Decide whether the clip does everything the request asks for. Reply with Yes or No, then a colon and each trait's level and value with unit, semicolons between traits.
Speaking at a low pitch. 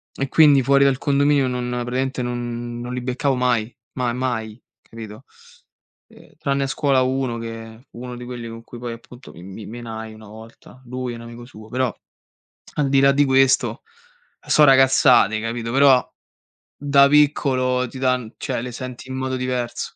Yes: low, 125 Hz